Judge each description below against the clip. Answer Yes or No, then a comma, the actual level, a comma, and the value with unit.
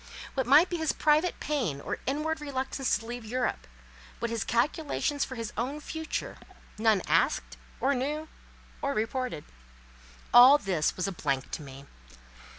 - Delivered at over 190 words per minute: No, average, 145 wpm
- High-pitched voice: Yes, very high, 255 Hz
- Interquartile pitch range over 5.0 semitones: Yes, wide, 5.4 semitones